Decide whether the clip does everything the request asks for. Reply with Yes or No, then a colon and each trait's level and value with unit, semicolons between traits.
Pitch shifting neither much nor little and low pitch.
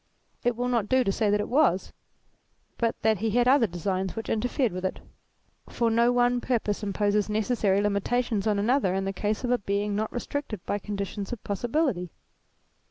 No: average, 3.3 semitones; high, 215 Hz